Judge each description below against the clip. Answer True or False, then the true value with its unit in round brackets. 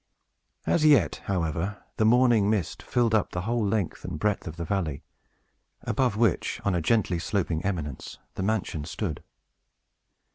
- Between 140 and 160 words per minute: True (150 wpm)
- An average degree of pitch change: True (4.8 semitones)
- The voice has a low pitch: True (100 Hz)